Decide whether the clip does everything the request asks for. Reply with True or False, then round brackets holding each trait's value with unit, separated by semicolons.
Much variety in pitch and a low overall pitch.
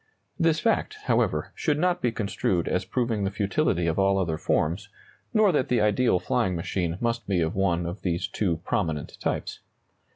True (6.1 semitones; 100 Hz)